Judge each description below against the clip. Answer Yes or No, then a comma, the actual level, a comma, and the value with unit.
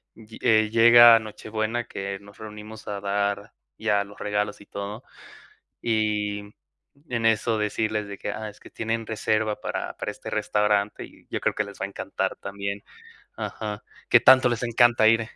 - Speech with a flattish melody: Yes, narrow, 1.6 semitones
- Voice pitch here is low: Yes, low, 105 Hz